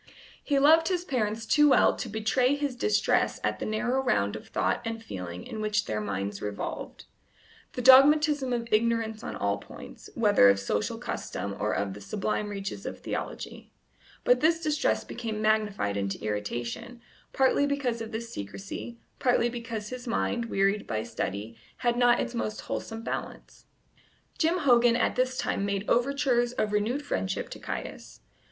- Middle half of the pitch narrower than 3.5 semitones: No, average, 4.5 semitones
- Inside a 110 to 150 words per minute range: No, average, 165 wpm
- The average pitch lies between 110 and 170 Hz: No, high, 230 Hz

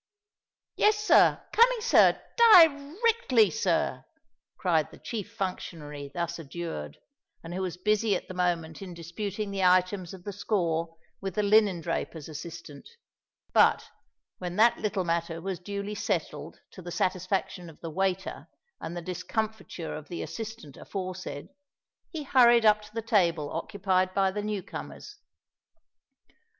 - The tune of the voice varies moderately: Yes, average, 3.9 semitones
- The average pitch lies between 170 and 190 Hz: Yes, medium, 185 Hz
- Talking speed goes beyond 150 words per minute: No, average, 140 wpm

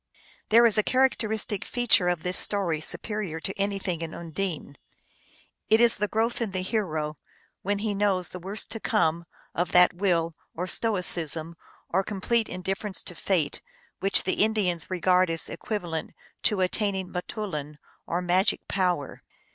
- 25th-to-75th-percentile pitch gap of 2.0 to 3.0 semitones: No, average, 3.4 semitones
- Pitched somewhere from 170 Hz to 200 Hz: Yes, medium, 185 Hz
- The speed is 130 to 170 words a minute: Yes, average, 155 wpm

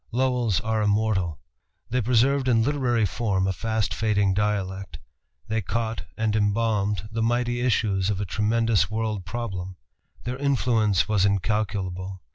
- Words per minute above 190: No, slow, 135 wpm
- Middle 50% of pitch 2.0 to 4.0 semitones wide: Yes, average, 3.0 semitones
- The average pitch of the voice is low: Yes, low, 110 Hz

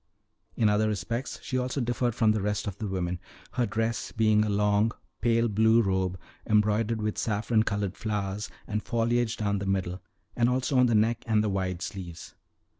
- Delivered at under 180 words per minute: No, average, 185 wpm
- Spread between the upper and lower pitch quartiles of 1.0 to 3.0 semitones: Yes, narrow, 2.4 semitones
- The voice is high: No, low, 105 Hz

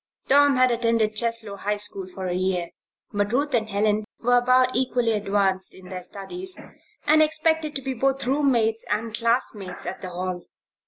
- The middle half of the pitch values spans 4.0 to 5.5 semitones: Yes, average, 4.5 semitones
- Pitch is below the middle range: No, high, 230 Hz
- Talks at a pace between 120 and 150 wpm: No, average, 170 wpm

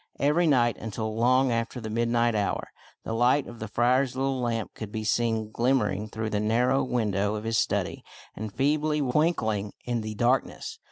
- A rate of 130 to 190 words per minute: Yes, average, 175 wpm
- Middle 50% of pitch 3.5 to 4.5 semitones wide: No, average, 2.8 semitones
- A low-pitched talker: Yes, low, 115 Hz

